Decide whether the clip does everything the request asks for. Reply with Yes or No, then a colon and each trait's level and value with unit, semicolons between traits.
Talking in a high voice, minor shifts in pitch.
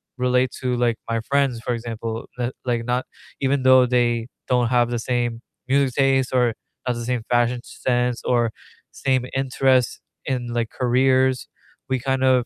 No: low, 125 Hz; narrow, 1.5 semitones